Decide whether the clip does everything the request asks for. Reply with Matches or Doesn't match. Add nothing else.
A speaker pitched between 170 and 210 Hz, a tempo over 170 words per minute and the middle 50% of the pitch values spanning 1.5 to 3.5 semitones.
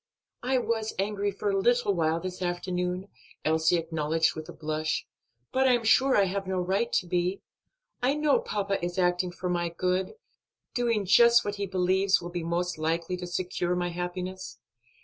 Matches